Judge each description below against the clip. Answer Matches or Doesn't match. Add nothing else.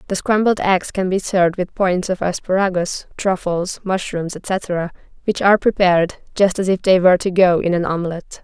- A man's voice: Doesn't match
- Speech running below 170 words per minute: Doesn't match